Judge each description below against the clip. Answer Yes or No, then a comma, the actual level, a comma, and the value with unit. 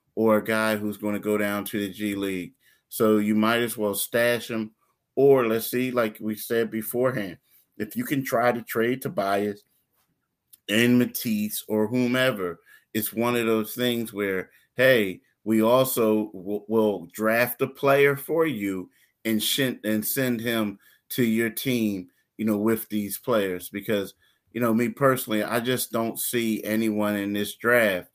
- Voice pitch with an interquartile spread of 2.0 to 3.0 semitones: Yes, narrow, 2.6 semitones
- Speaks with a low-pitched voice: Yes, low, 110 Hz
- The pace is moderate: Yes, average, 170 wpm